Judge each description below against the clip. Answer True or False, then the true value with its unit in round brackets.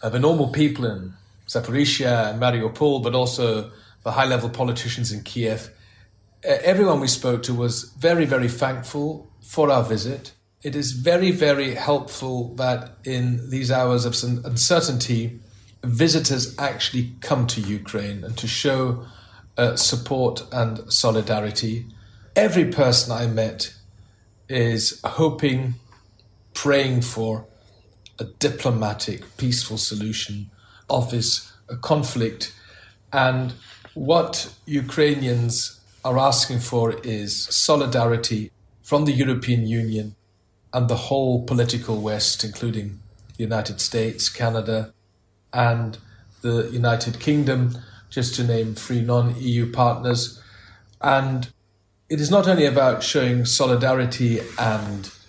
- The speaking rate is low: True (115 wpm)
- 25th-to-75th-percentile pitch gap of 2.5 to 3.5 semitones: True (3.1 semitones)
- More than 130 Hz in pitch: False (120 Hz)